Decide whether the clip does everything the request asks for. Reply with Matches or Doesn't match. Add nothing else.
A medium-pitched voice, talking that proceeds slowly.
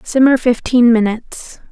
Doesn't match